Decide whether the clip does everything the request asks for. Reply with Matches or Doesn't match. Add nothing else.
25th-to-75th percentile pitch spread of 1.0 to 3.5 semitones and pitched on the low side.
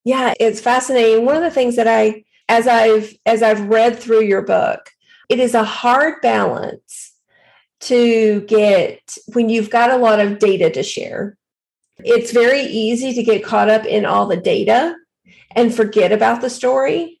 Doesn't match